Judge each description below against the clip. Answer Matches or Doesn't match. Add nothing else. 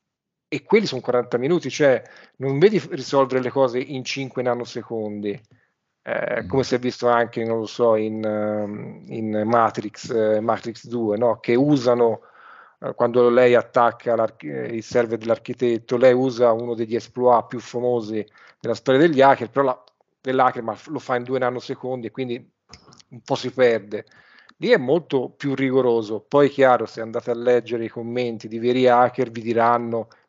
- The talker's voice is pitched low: Matches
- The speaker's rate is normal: Matches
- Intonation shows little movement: Matches